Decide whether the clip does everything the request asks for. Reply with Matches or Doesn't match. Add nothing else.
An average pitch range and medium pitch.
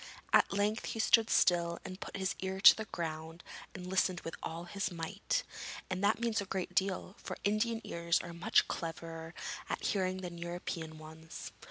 Matches